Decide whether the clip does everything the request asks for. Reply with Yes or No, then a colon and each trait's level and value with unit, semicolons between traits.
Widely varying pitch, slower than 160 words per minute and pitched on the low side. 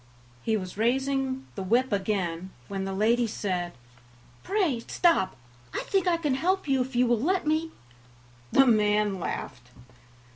No: wide, 6.0 semitones; average, 150 wpm; high, 235 Hz